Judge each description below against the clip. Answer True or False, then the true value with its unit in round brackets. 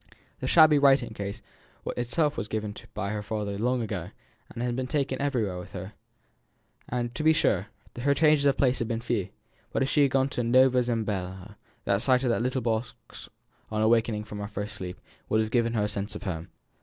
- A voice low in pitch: True (115 Hz)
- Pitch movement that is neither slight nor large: True (3.8 semitones)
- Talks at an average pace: False (220 wpm)